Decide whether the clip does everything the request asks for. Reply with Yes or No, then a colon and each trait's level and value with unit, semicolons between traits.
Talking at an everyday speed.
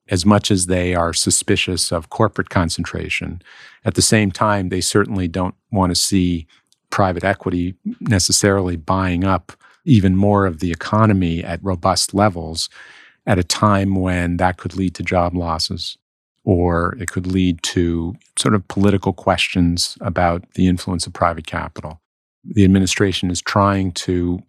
Yes: average, 150 wpm